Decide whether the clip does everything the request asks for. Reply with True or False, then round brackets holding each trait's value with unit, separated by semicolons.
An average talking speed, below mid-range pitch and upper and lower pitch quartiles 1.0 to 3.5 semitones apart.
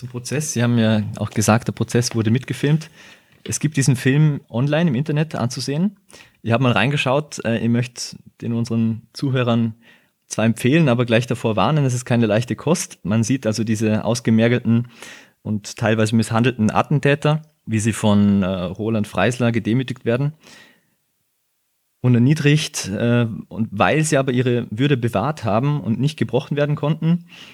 False (150 wpm; 120 Hz; 4.3 semitones)